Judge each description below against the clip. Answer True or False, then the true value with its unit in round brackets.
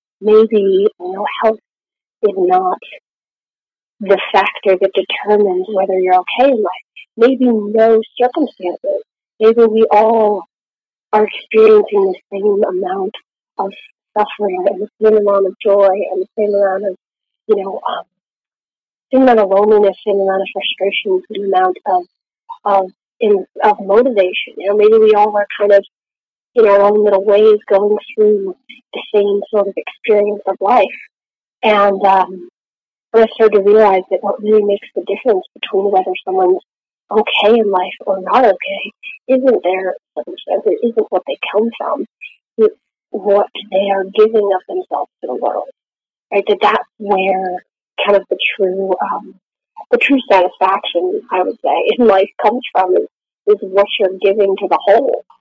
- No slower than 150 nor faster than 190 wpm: True (160 wpm)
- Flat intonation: False (4.2 semitones)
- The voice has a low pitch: False (210 Hz)